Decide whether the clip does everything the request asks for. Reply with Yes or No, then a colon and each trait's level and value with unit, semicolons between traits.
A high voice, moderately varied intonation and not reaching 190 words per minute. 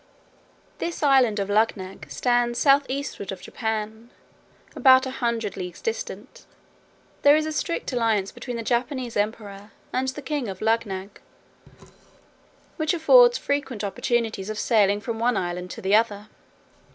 Yes: high, 230 Hz; average, 4.5 semitones; average, 140 wpm